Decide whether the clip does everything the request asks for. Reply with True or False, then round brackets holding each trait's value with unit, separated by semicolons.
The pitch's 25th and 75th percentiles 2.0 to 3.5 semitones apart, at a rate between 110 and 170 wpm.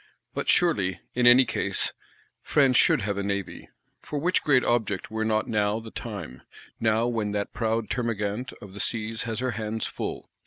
False (2.9 semitones; 180 wpm)